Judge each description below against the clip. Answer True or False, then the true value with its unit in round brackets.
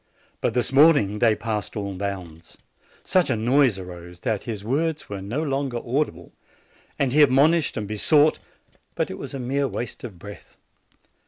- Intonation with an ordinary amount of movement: False (5.7 semitones)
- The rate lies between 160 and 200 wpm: True (165 wpm)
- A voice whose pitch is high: False (120 Hz)